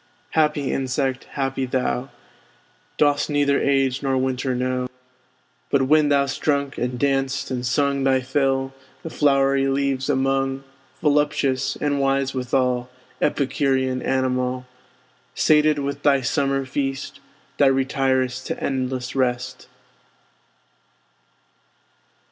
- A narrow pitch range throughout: Yes, narrow, 1.3 semitones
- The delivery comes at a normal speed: No, slow, 110 wpm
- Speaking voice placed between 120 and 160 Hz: Yes, low, 135 Hz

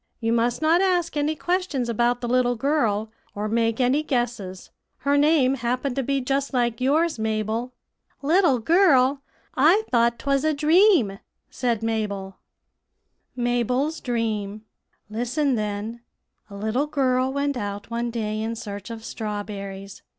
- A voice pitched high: Yes, high, 245 Hz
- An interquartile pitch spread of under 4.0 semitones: No, average, 4.3 semitones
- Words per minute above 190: No, average, 145 wpm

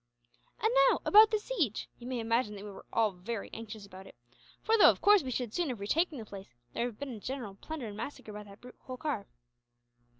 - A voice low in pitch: No, high, 235 Hz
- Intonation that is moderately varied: No, wide, 5.7 semitones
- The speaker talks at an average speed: No, fast, 235 wpm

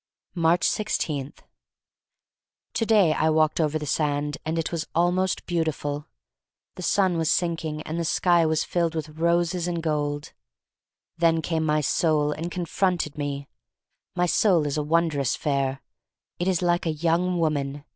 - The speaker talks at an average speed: Yes, average, 150 wpm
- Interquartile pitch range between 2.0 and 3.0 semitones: Yes, narrow, 2.4 semitones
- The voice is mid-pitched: Yes, medium, 160 Hz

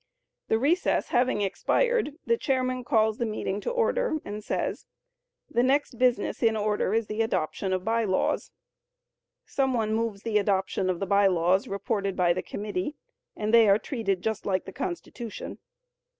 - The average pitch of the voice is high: Yes, high, 215 Hz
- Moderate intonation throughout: Yes, average, 3.9 semitones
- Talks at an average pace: Yes, average, 165 wpm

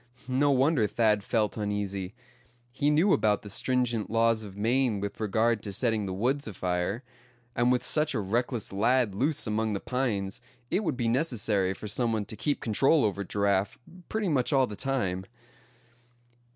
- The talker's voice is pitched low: Yes, low, 110 Hz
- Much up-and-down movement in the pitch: No, average, 4.1 semitones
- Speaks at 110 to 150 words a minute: No, average, 170 wpm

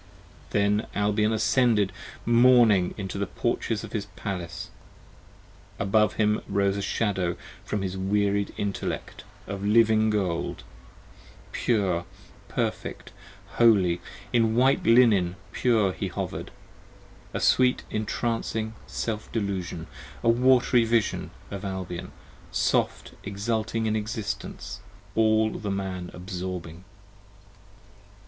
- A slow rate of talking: Yes, slow, 105 wpm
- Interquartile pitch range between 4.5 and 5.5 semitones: No, average, 2.8 semitones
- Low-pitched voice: Yes, low, 105 Hz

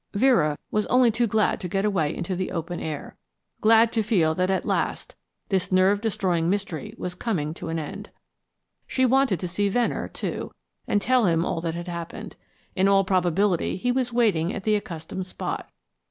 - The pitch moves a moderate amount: Yes, average, 4.0 semitones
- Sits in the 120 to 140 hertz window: No, high, 190 Hz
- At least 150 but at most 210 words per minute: Yes, average, 185 wpm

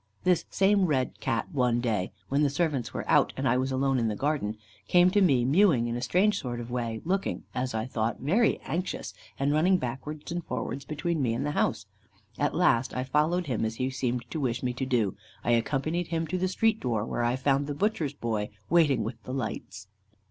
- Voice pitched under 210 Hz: Yes, low, 135 Hz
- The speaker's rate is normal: No, fast, 215 wpm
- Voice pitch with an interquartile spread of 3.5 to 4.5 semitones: No, wide, 5.5 semitones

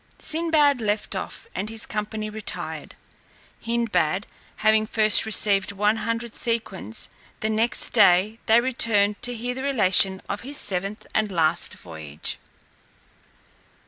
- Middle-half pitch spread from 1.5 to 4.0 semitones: Yes, average, 2.8 semitones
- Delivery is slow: Yes, slow, 125 wpm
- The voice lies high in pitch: Yes, high, 215 Hz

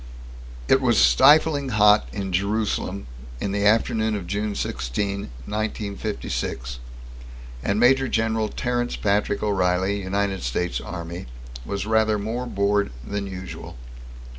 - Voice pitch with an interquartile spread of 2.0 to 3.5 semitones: Yes, average, 2.7 semitones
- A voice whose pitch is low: Yes, low, 100 Hz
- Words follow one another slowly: Yes, slow, 120 wpm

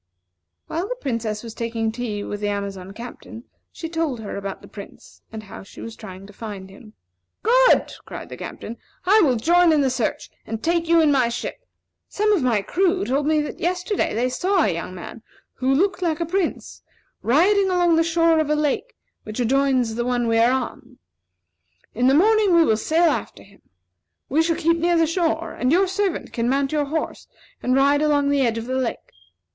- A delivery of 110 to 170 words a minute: No, fast, 205 wpm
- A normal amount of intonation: No, wide, 6.7 semitones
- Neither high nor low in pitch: No, very high, 275 Hz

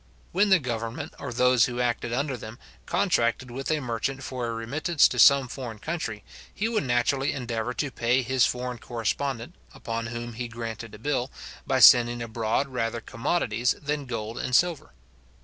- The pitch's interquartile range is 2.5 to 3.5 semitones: Yes, average, 2.8 semitones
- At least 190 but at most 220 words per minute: No, average, 170 wpm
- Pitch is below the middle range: Yes, low, 125 Hz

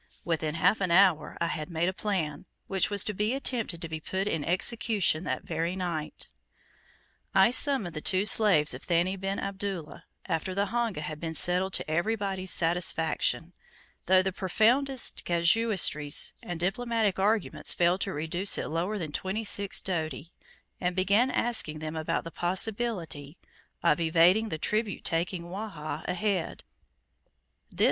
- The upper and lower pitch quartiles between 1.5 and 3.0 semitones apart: No, average, 3.7 semitones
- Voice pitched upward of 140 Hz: Yes, medium, 185 Hz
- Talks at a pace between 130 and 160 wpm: Yes, average, 150 wpm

